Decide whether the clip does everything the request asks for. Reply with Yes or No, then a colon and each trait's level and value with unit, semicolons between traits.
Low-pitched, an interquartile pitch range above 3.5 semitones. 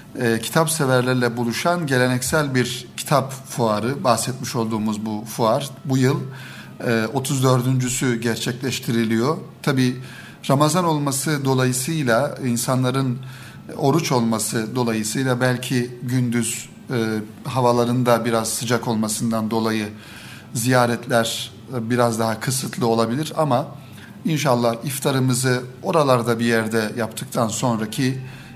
No: low, 125 Hz; narrow, 2.4 semitones